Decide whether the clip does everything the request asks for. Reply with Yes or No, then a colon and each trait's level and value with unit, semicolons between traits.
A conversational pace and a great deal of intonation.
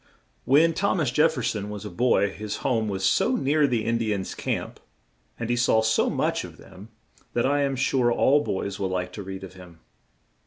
No: fast, 220 wpm; wide, 5.7 semitones